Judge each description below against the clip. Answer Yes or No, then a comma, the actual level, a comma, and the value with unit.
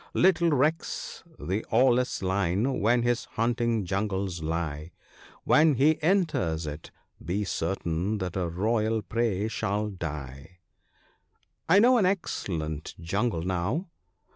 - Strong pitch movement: Yes, wide, 6.1 semitones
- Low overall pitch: Yes, low, 105 Hz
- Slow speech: Yes, slow, 125 wpm